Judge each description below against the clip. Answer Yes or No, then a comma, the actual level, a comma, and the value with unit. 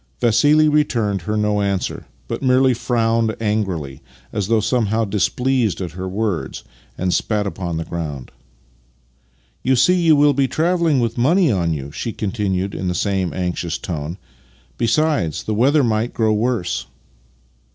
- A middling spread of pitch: No, wide, 5.7 semitones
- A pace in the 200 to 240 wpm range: No, average, 160 wpm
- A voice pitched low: Yes, low, 105 Hz